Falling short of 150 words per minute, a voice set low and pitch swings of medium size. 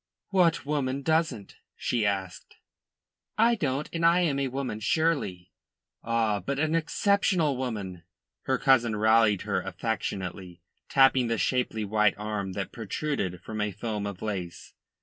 No: average, 140 wpm; low, 115 Hz; wide, 5.9 semitones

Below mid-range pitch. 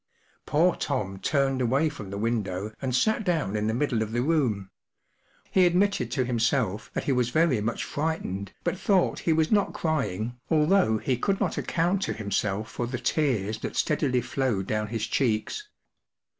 Yes: low, 125 Hz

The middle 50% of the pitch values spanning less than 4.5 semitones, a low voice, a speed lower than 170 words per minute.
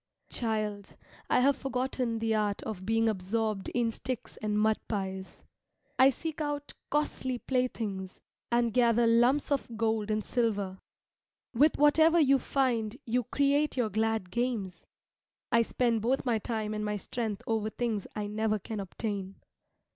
No: average, 3.1 semitones; high, 225 Hz; average, 145 wpm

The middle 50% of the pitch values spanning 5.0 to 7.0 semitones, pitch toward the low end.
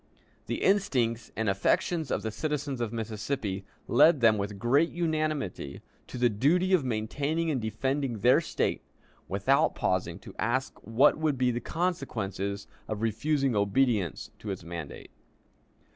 Yes: wide, 5.6 semitones; low, 120 Hz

